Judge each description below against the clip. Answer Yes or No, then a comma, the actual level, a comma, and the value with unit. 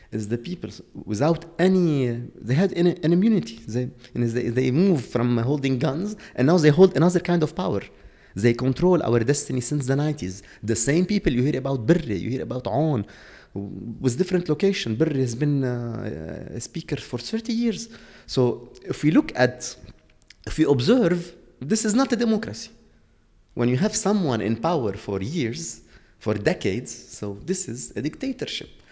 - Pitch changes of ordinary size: No, wide, 6.9 semitones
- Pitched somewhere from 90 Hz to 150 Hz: Yes, medium, 140 Hz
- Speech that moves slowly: No, average, 180 wpm